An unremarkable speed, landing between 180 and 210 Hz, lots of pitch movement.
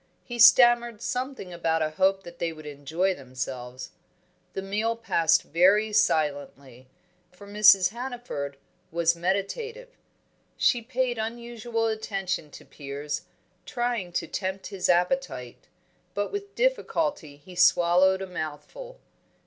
No: slow, 120 wpm; high, 190 Hz; wide, 6.8 semitones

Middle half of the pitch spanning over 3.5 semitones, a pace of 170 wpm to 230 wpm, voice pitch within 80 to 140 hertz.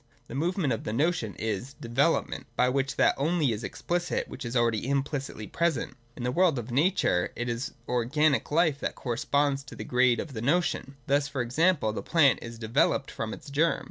Yes: average, 4.4 semitones; average, 180 wpm; low, 135 Hz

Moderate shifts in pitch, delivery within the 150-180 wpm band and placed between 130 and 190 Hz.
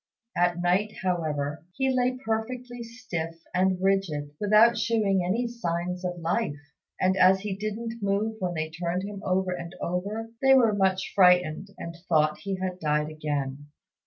Yes: average, 4.1 semitones; average, 160 wpm; medium, 185 Hz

